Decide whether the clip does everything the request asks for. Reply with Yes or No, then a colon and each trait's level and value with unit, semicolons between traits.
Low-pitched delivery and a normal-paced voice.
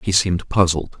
Yes: very low, 90 Hz; average, 180 wpm